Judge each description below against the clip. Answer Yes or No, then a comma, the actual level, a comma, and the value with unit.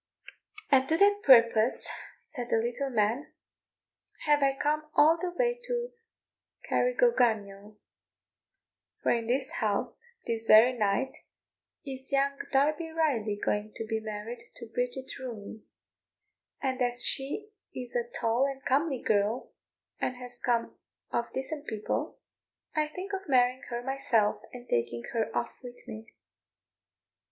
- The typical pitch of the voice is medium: No, very high, 250 Hz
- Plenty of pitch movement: No, average, 4.0 semitones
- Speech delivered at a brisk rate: No, slow, 135 wpm